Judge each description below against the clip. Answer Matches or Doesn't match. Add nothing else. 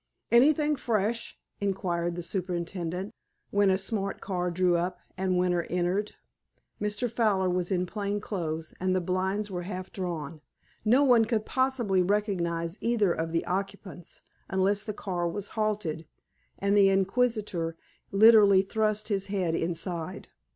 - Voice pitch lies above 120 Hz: Matches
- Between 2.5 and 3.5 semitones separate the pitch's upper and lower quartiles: Matches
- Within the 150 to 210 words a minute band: Doesn't match